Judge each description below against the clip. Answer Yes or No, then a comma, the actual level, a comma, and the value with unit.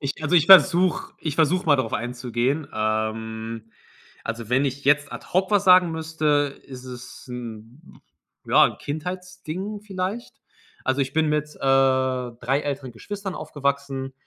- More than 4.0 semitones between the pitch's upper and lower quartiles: Yes, average, 4.9 semitones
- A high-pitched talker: No, medium, 140 Hz